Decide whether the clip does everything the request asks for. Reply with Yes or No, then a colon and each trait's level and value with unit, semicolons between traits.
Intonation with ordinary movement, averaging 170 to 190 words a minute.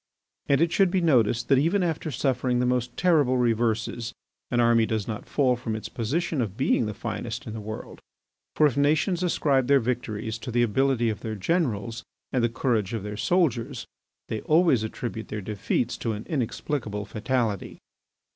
Yes: average, 4.1 semitones; average, 180 wpm